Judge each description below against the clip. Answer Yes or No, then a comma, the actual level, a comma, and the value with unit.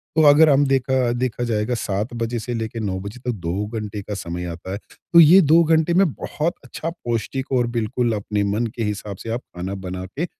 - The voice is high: No, low, 120 Hz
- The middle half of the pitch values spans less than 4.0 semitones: No, average, 4.8 semitones